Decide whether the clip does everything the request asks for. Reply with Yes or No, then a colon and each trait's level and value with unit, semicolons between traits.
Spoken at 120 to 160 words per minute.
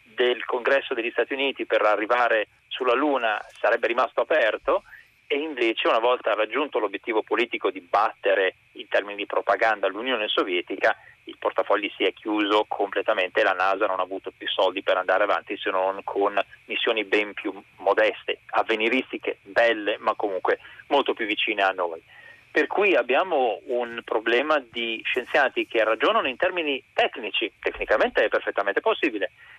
Yes: average, 150 wpm